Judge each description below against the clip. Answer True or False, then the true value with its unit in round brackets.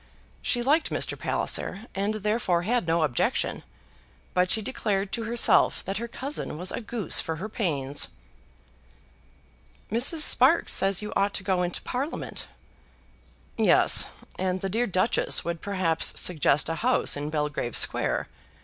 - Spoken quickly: False (145 wpm)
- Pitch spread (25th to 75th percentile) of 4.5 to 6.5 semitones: True (5.1 semitones)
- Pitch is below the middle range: False (195 Hz)